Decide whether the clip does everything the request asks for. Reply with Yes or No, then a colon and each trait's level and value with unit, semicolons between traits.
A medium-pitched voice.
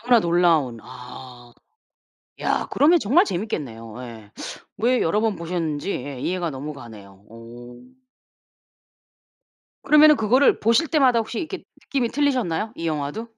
Yes: medium, 170 Hz